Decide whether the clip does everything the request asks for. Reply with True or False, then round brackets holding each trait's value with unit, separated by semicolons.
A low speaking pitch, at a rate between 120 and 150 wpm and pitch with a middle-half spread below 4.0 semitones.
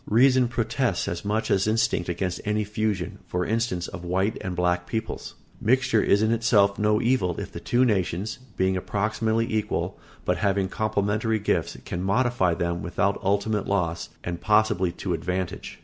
False (100 Hz; 165 wpm; 3.4 semitones)